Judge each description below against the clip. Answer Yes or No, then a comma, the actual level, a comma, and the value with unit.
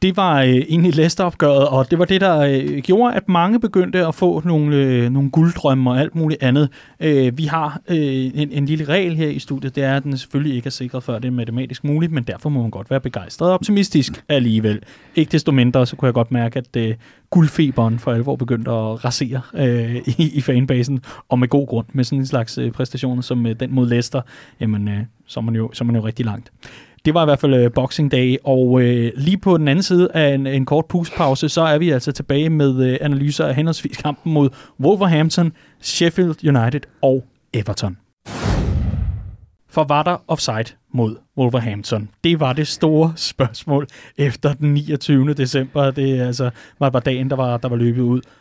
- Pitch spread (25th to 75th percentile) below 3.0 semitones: No, average, 3.7 semitones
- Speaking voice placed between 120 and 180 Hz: Yes, low, 135 Hz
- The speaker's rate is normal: Yes, average, 205 wpm